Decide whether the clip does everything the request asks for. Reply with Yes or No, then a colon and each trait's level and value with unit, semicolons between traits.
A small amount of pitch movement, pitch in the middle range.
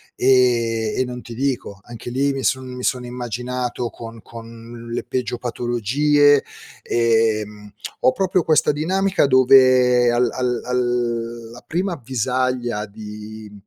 No: narrow, 2.0 semitones; low, 125 Hz